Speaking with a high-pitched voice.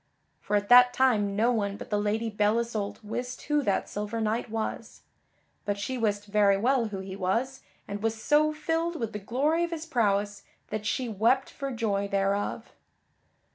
Yes: high, 220 Hz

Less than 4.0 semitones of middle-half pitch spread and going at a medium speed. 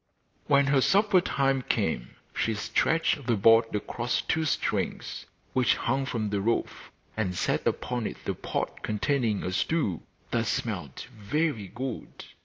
No: average, 4.8 semitones; average, 145 wpm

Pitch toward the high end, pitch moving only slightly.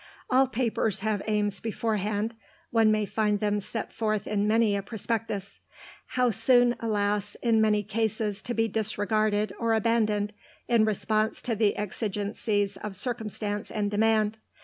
Yes: high, 215 Hz; narrow, 1.5 semitones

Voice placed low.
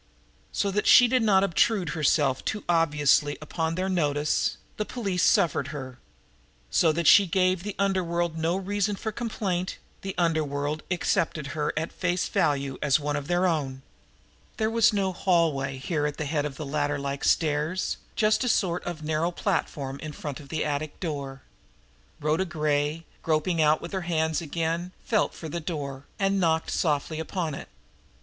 No: medium, 160 Hz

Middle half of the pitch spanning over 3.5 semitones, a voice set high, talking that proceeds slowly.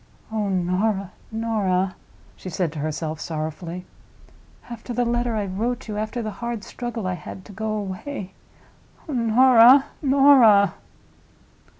Yes: average, 4.4 semitones; high, 215 Hz; slow, 125 wpm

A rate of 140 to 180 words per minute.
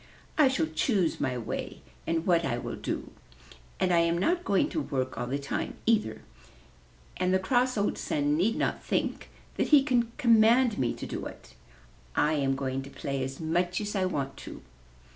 No: average, 190 wpm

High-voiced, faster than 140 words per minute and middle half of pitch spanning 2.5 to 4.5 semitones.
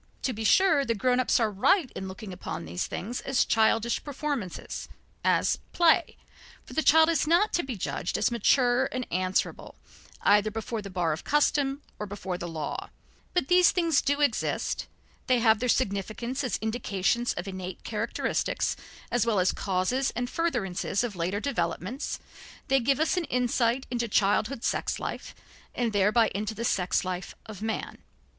No: high, 230 Hz; average, 170 wpm; wide, 5.5 semitones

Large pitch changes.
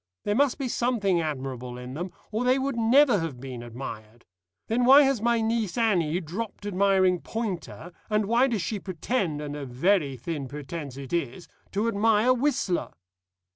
Yes: wide, 7.8 semitones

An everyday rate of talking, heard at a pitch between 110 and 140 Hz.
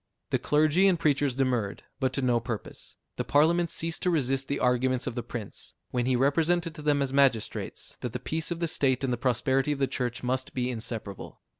No: fast, 210 wpm; low, 135 Hz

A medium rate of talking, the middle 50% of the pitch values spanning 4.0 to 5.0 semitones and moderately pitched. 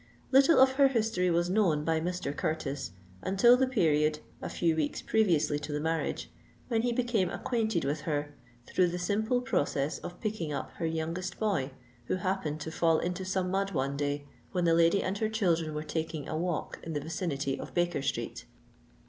Yes: average, 190 wpm; average, 4.5 semitones; medium, 170 Hz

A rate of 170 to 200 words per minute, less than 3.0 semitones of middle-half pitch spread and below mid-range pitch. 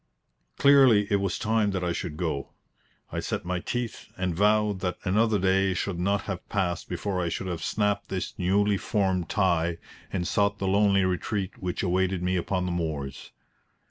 Yes: average, 175 wpm; narrow, 2.4 semitones; very low, 95 Hz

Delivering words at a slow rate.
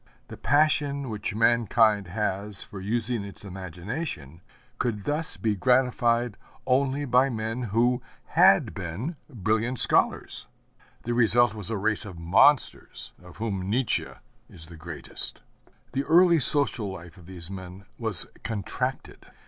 Yes: slow, 130 wpm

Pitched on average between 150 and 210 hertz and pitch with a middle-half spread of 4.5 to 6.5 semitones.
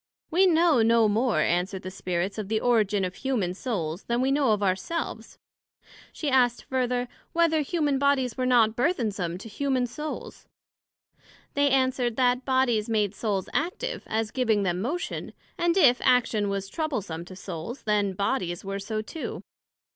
No: high, 235 Hz; average, 5.2 semitones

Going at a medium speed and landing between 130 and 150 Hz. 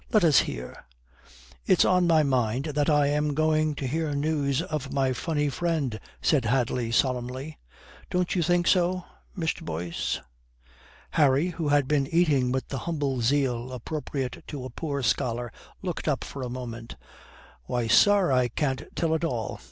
Yes: average, 160 wpm; medium, 140 Hz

